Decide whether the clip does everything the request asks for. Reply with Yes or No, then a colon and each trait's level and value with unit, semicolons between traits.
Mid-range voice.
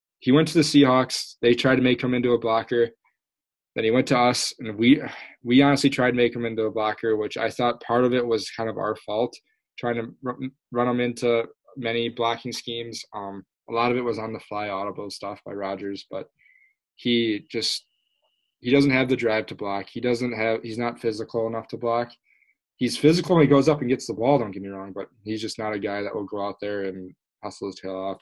No: low, 115 Hz